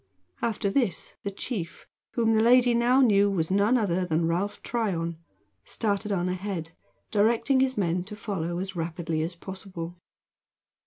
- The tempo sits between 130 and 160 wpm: Yes, average, 150 wpm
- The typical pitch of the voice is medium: No, high, 195 Hz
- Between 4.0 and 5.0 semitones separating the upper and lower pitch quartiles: Yes, average, 4.5 semitones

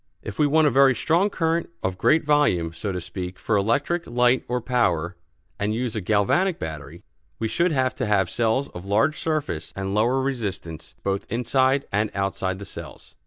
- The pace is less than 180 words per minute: No, average, 185 wpm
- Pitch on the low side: Yes, low, 115 Hz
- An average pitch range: No, wide, 6.3 semitones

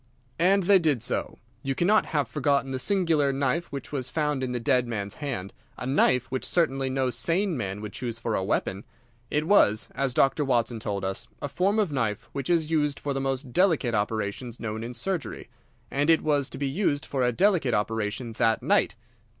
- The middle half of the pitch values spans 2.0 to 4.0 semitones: No, average, 4.6 semitones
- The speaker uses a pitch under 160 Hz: Yes, low, 135 Hz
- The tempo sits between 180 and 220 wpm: Yes, average, 200 wpm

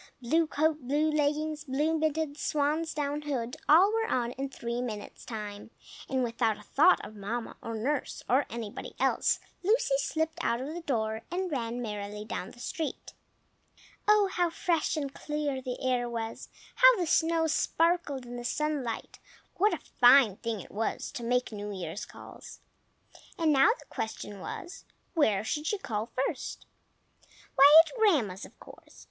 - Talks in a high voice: Yes, very high, 275 Hz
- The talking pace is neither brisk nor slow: Yes, average, 165 wpm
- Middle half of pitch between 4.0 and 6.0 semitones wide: Yes, average, 5.3 semitones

